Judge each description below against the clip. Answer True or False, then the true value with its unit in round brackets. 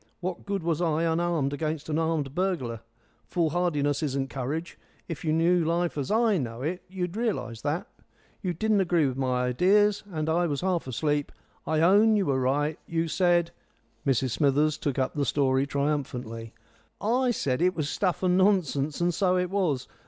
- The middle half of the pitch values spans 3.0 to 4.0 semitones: False (4.4 semitones)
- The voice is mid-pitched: True (160 Hz)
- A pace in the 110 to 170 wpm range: False (180 wpm)